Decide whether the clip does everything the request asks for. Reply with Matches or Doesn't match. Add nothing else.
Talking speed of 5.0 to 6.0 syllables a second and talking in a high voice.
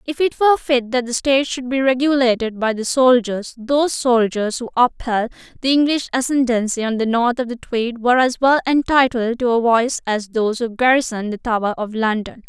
Matches